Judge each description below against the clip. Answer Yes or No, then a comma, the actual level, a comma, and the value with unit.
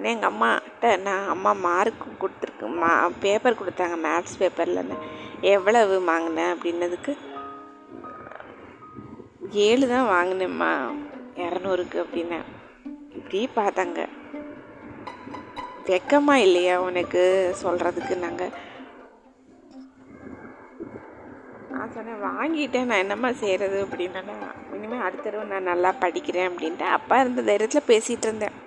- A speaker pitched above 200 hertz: No, high, 195 Hz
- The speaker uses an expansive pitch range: Yes, wide, 6.2 semitones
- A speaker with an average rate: Yes, average, 95 wpm